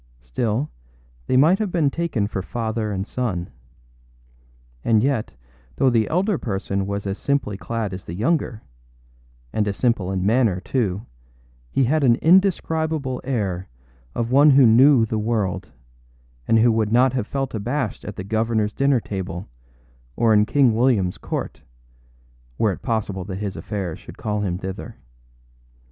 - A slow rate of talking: No, average, 155 wpm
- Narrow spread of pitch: No, average, 4.8 semitones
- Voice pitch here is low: Yes, low, 110 Hz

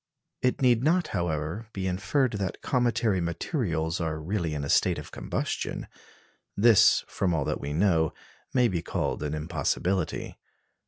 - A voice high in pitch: No, very low, 95 Hz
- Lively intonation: Yes, wide, 6.2 semitones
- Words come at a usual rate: Yes, average, 150 wpm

